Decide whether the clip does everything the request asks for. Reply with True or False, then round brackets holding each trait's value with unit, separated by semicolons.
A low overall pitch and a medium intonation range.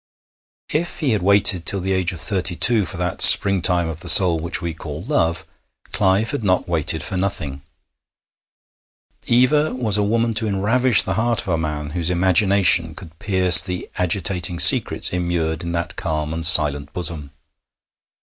True (90 Hz; 3.6 semitones)